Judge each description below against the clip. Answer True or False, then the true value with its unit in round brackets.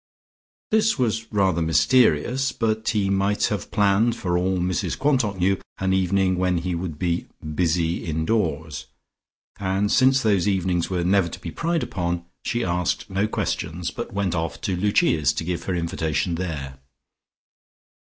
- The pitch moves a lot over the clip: False (3.4 semitones)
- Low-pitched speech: True (95 Hz)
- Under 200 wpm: True (155 wpm)